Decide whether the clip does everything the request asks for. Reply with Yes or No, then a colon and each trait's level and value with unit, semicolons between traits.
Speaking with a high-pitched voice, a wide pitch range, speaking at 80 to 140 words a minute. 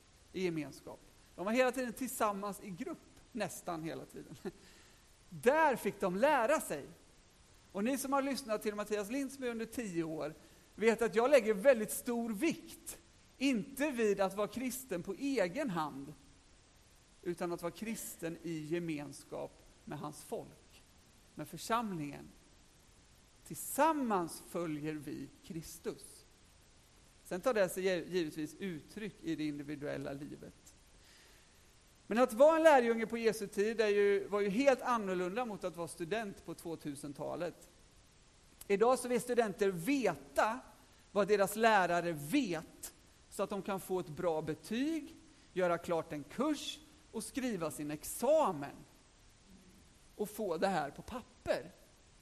Yes: high, 200 Hz; wide, 6.6 semitones; average, 135 wpm